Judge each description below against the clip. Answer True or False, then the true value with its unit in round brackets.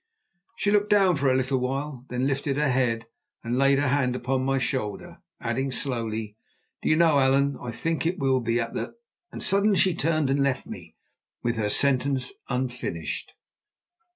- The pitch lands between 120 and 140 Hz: True (135 Hz)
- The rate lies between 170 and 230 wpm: True (180 wpm)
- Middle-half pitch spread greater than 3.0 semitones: False (2.4 semitones)